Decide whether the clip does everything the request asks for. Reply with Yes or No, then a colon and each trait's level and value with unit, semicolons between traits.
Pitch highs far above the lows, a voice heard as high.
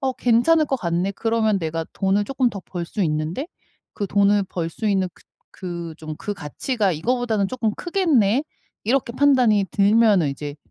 Yes: wide, 5.7 semitones; high, 205 Hz